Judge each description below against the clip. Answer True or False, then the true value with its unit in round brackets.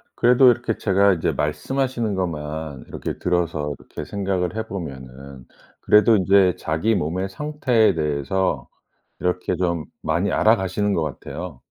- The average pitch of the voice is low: True (90 Hz)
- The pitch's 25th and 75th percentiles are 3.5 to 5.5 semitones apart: True (5.2 semitones)